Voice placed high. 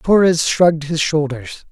No: medium, 155 Hz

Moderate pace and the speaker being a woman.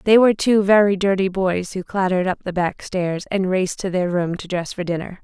No: fast, 240 wpm; female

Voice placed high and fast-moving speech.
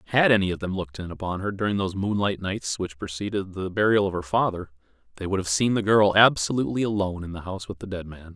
No: very low, 95 Hz; fast, 245 wpm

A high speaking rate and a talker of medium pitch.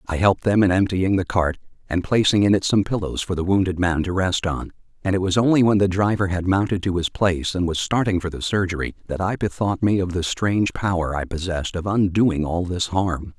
No: fast, 240 wpm; very low, 95 Hz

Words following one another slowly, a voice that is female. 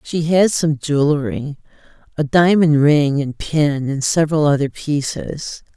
Yes: slow, 125 wpm; female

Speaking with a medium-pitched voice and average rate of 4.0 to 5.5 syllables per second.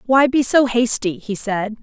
No: high, 235 Hz; 4.2 syllables/s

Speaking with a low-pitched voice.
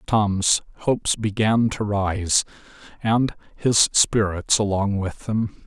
Yes: low, 105 Hz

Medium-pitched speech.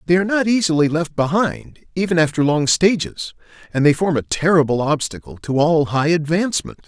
Yes: medium, 160 Hz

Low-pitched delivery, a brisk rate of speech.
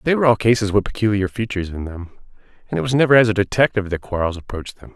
Yes: low, 105 Hz; fast, 240 wpm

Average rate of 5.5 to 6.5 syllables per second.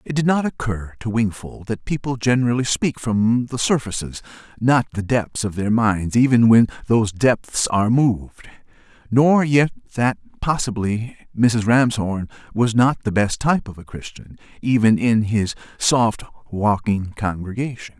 No: 4.5 syllables/s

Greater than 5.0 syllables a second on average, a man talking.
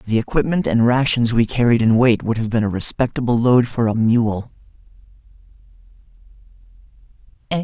Yes: 5.4 syllables/s; male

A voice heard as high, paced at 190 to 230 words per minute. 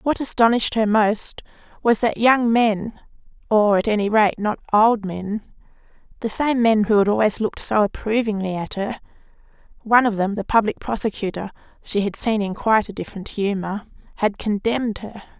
No: high, 215 Hz; average, 155 wpm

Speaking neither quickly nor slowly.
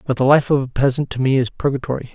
No: fast, 280 wpm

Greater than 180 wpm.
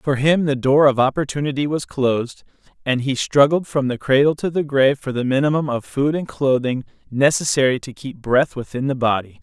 Yes: average, 195 wpm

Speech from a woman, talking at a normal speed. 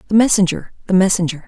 Yes: female; average, 165 wpm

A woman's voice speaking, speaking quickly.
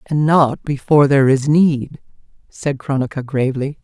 No: female; average, 140 wpm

